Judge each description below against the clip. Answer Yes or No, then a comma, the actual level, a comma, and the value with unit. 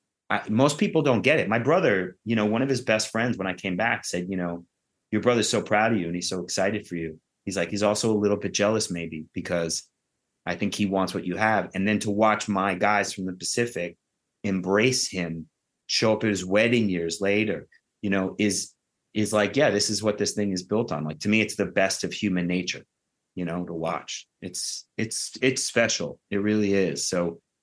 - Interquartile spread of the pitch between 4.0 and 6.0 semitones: No, average, 2.9 semitones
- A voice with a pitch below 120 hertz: Yes, low, 100 Hz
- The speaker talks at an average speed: No, fast, 225 wpm